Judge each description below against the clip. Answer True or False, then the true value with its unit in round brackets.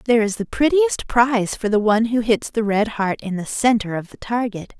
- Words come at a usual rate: False (240 wpm)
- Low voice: False (225 Hz)